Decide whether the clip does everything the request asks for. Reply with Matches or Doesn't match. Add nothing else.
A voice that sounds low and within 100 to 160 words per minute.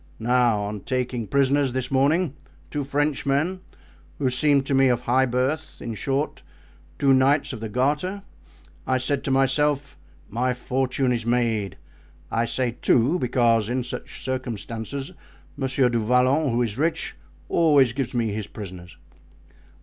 Matches